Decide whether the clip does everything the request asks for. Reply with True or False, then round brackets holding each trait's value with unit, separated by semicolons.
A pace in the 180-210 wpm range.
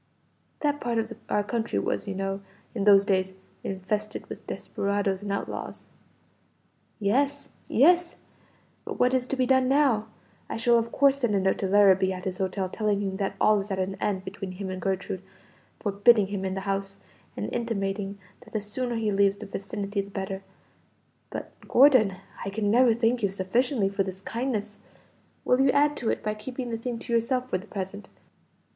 True (185 wpm)